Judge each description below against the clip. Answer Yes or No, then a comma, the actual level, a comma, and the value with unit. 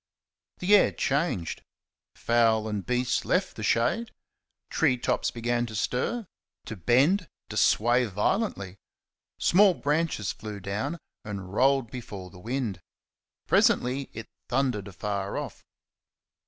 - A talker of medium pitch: No, low, 120 Hz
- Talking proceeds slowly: Yes, slow, 120 wpm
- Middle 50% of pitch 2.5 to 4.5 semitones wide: No, average, 5.1 semitones